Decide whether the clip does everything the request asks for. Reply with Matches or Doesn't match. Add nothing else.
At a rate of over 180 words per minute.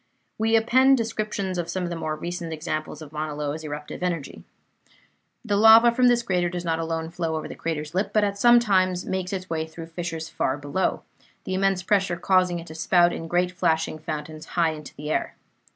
Matches